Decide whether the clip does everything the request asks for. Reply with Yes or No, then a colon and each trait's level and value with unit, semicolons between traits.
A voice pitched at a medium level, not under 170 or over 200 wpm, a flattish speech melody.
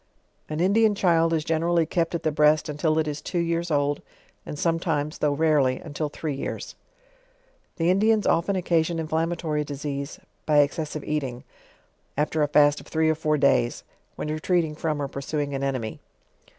Yes: medium, 155 Hz; average, 175 wpm; narrow, 2.2 semitones